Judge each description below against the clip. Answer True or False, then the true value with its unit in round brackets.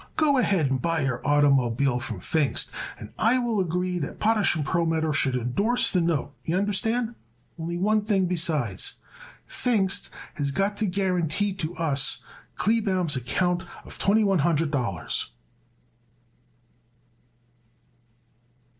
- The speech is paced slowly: True (125 wpm)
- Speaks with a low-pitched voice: False (175 Hz)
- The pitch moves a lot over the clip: True (5.8 semitones)